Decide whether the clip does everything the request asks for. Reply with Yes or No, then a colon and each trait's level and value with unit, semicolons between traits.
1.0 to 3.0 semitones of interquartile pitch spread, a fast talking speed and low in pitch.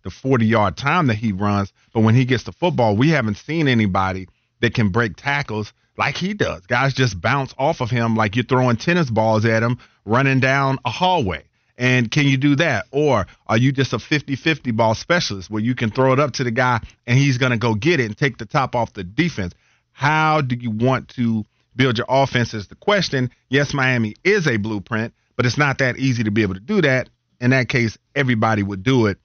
No: average, 3.5 semitones; fast, 225 wpm; low, 125 Hz